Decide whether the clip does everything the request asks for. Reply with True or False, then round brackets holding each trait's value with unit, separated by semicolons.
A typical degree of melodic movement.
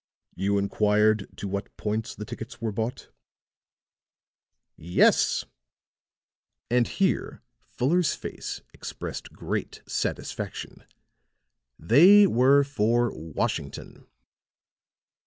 True (4.6 semitones)